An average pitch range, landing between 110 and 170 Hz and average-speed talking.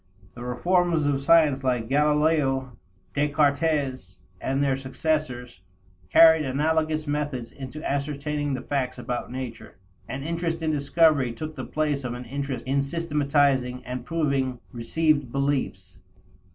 No: average, 3.1 semitones; medium, 140 Hz; slow, 125 wpm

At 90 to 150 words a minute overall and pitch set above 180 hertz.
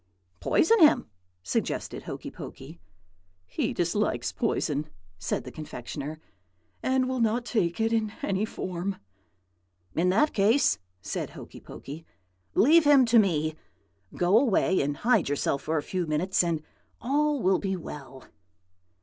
Yes: slow, 135 wpm; high, 190 Hz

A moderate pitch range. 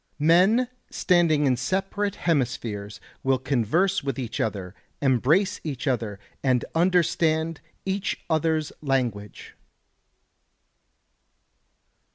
No: wide, 5.7 semitones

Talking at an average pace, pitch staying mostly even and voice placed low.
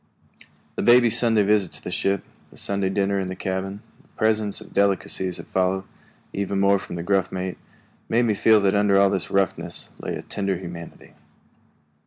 Yes: average, 180 wpm; narrow, 1.6 semitones; low, 100 Hz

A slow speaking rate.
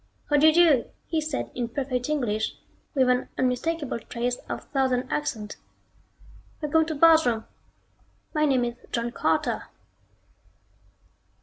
Yes: slow, 125 wpm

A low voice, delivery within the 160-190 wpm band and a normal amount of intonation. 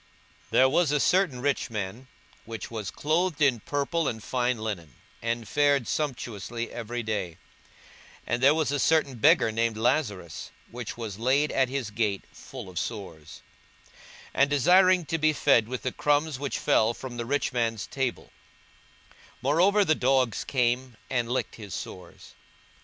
Yes: low, 125 Hz; average, 165 wpm; average, 4.2 semitones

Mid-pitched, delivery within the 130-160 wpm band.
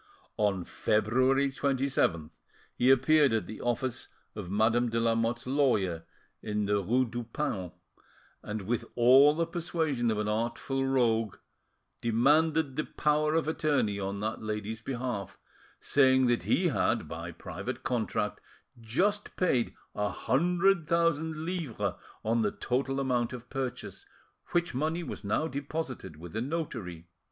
No: low, 125 Hz; average, 140 wpm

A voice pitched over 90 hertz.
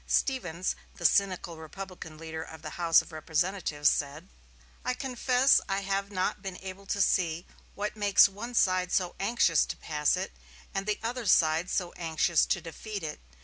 Yes: medium, 185 Hz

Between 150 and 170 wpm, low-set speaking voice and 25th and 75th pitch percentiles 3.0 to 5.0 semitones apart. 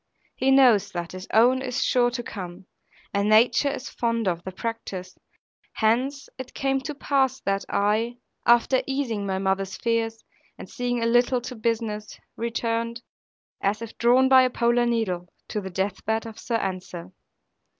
No: average, 165 wpm; high, 230 Hz; average, 3.6 semitones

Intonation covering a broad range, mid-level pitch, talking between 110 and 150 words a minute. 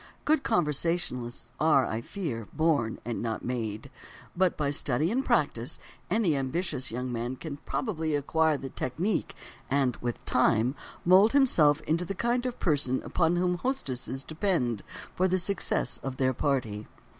Yes: wide, 5.9 semitones; medium, 150 Hz; average, 145 wpm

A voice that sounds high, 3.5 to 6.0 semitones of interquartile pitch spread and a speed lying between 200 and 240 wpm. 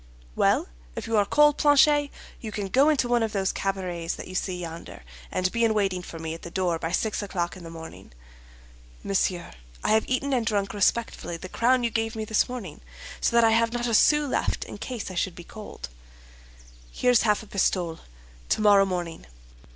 Yes: high, 205 Hz; average, 4.6 semitones; fast, 205 wpm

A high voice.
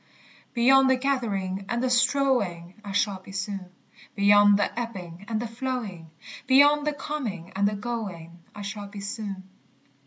Yes: high, 205 Hz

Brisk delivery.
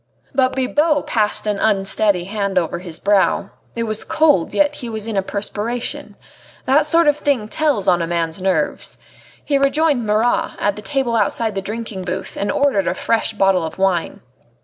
No: average, 180 wpm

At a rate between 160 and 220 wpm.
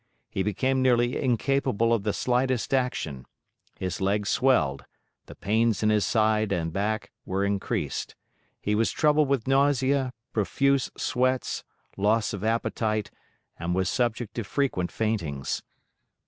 No: slow, 135 wpm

